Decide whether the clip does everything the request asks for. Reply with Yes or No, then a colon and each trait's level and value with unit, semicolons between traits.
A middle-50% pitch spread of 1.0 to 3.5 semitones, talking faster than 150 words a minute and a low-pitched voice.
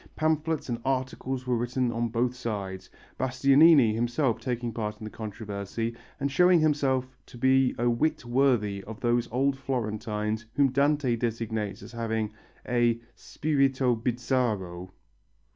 No: average, 3.1 semitones; slow, 135 wpm; low, 120 Hz